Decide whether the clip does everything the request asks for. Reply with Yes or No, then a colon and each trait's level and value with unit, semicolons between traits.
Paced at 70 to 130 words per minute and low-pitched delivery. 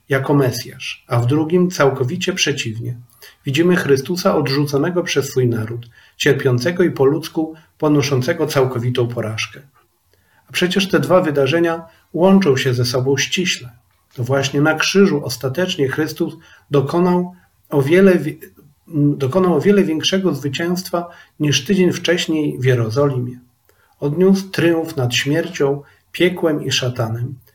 No: average, 120 wpm; medium, 145 Hz